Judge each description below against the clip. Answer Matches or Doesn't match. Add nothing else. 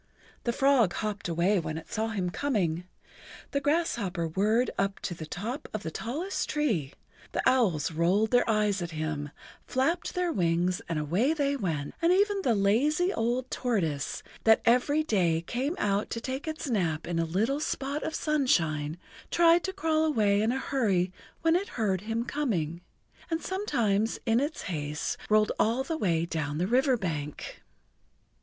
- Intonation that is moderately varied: Doesn't match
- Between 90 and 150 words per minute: Doesn't match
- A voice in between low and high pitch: Doesn't match